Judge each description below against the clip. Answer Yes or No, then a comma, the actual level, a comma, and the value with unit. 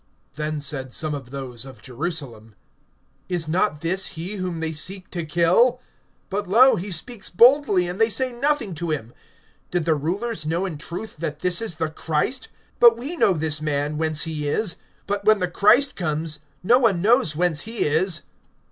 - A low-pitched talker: No, medium, 170 Hz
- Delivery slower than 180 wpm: No, average, 185 wpm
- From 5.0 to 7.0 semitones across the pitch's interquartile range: Yes, wide, 5.5 semitones